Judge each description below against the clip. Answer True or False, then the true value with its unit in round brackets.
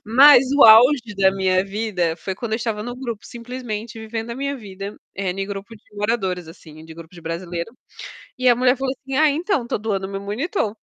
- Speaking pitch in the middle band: False (220 Hz)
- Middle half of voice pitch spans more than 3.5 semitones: True (4.4 semitones)